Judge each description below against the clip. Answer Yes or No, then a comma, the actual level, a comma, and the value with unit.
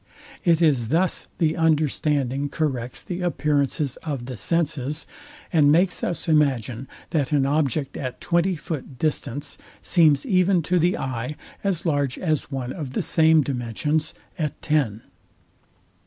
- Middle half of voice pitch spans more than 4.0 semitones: No, average, 3.5 semitones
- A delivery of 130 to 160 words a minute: Yes, average, 140 wpm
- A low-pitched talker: No, medium, 150 Hz